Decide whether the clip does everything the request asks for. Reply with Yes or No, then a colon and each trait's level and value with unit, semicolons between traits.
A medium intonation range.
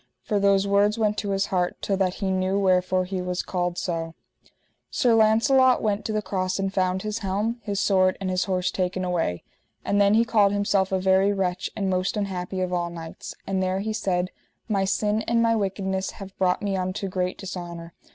No: narrow, 1.9 semitones